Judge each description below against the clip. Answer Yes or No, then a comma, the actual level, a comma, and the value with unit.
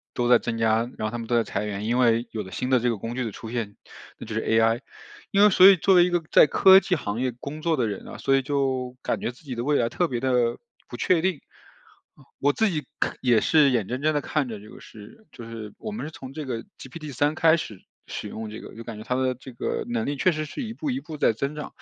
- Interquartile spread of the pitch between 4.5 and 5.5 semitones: Yes, average, 5.1 semitones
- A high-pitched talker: No, low, 125 Hz